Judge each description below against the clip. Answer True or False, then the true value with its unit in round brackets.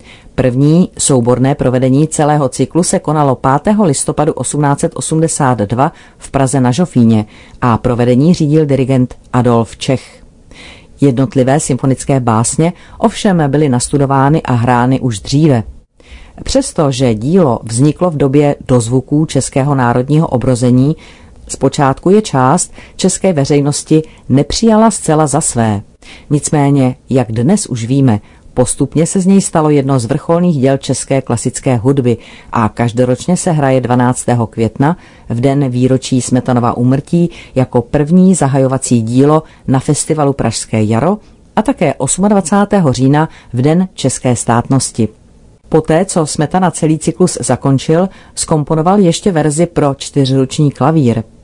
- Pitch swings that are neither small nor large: True (4.0 semitones)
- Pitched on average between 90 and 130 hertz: False (140 Hz)